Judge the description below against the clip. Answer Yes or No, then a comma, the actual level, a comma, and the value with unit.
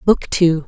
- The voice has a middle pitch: Yes, medium, 170 Hz